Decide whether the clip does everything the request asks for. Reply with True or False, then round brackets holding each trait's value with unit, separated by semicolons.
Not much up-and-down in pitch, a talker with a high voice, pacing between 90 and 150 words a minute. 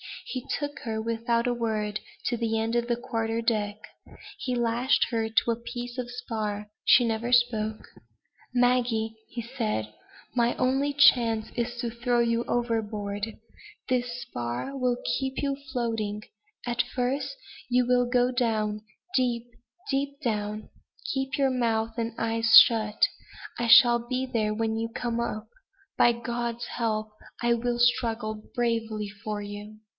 True (1.9 semitones; 235 Hz; 145 wpm)